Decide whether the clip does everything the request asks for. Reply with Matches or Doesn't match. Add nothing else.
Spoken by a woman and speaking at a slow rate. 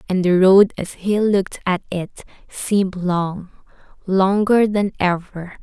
Matches